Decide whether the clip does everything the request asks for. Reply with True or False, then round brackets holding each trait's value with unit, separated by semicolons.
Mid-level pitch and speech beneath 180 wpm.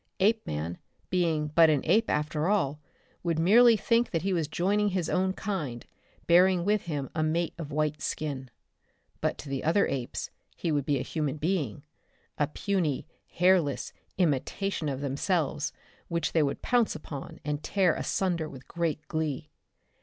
True (160 Hz; 160 wpm)